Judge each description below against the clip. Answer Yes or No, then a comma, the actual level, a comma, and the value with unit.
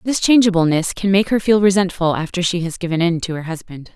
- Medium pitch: Yes, medium, 180 Hz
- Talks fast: Yes, fast, 230 wpm